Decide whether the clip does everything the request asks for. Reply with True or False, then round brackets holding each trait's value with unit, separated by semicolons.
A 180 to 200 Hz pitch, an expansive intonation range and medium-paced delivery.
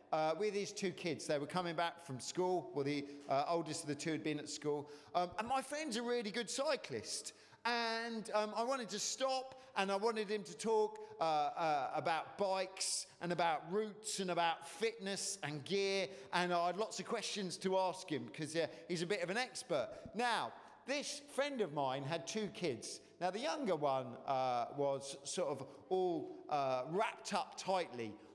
True (190 Hz; 5.7 semitones; 195 wpm)